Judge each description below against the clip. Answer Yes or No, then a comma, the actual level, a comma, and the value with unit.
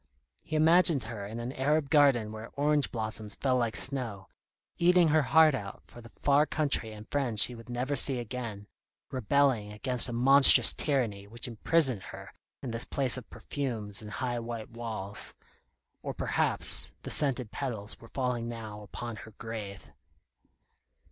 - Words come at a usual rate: Yes, average, 160 wpm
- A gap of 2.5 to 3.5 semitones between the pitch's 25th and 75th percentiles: No, average, 4.1 semitones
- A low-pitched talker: Yes, low, 120 Hz